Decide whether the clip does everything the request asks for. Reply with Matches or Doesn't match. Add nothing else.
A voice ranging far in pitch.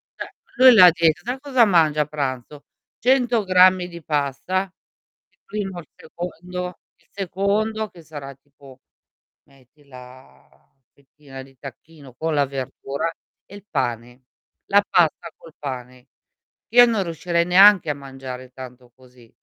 Matches